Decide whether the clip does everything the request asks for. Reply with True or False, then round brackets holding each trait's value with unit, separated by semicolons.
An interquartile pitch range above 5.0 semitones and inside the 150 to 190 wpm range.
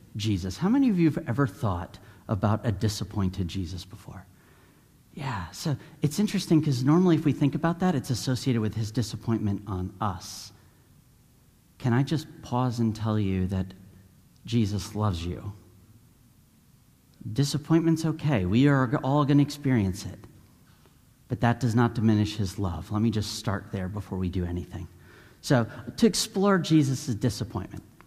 True (5.6 semitones; 155 wpm)